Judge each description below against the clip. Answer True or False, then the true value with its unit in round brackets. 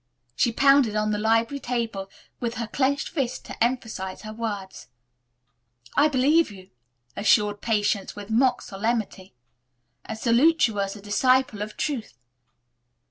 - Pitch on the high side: True (225 Hz)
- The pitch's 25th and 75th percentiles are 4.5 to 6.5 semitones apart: False (3.7 semitones)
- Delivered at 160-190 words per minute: False (135 wpm)